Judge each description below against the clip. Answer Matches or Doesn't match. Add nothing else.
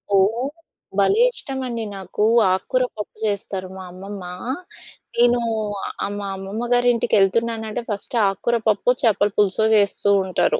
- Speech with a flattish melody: Doesn't match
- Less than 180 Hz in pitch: Doesn't match